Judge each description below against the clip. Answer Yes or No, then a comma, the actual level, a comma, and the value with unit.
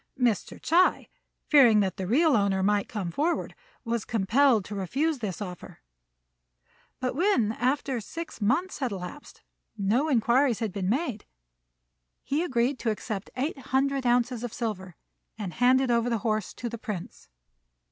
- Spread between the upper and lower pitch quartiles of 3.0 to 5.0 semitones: Yes, average, 4.7 semitones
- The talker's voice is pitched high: Yes, high, 235 Hz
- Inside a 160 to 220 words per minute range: No, average, 150 wpm